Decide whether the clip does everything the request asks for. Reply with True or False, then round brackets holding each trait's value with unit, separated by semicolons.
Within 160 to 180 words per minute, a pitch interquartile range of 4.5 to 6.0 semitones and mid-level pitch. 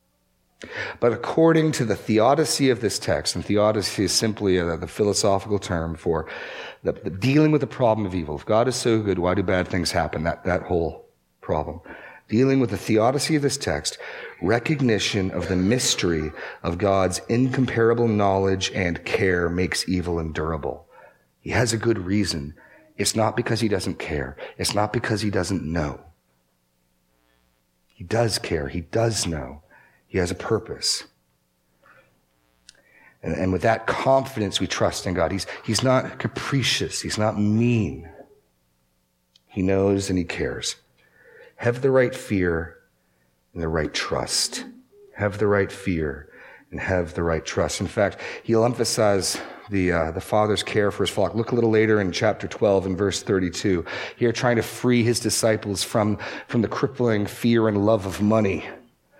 False (165 wpm; 5.3 semitones; 100 Hz)